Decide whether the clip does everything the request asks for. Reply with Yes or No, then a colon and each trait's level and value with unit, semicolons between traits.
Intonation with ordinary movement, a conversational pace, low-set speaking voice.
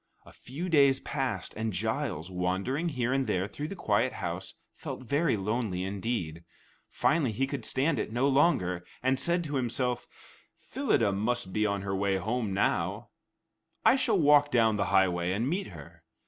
No: wide, 6.4 semitones; average, 170 wpm; low, 120 Hz